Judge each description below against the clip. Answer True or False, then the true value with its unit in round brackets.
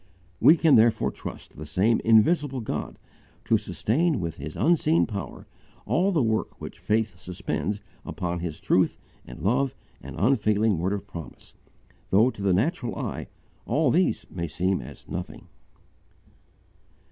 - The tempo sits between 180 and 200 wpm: False (145 wpm)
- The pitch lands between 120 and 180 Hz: False (105 Hz)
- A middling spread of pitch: False (6.9 semitones)